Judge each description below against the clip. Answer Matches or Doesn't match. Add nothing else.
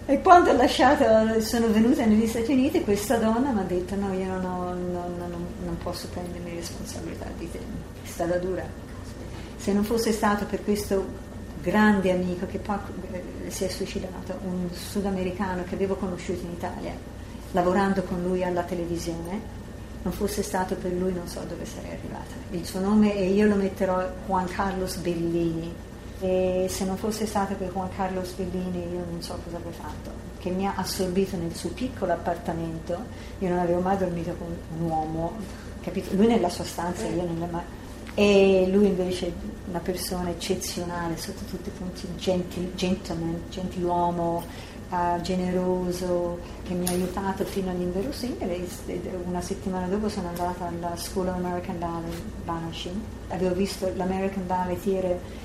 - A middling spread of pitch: Doesn't match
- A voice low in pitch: Doesn't match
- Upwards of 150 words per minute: Matches